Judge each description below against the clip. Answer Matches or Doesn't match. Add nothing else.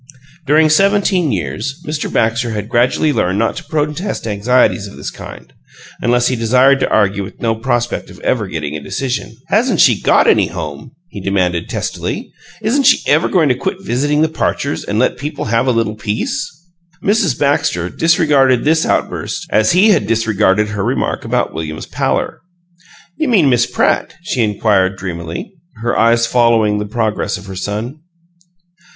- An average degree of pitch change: Doesn't match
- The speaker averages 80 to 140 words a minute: Doesn't match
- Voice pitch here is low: Matches